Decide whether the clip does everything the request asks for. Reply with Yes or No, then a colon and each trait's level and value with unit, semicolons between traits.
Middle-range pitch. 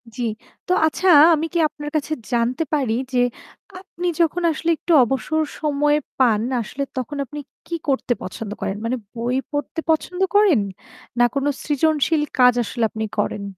No: very high, 290 Hz